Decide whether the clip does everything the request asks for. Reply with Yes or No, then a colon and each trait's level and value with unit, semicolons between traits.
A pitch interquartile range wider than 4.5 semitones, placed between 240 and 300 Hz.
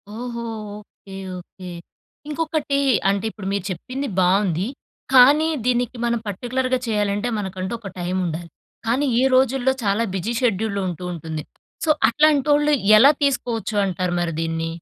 No: wide, 5.6 semitones; high, 220 Hz